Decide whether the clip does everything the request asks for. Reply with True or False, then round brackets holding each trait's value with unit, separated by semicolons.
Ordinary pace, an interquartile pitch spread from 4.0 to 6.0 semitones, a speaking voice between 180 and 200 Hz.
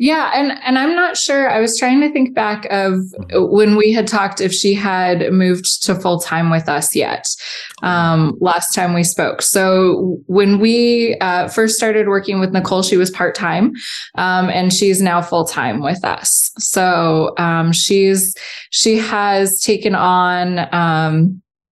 False (170 wpm; 3.2 semitones; 190 Hz)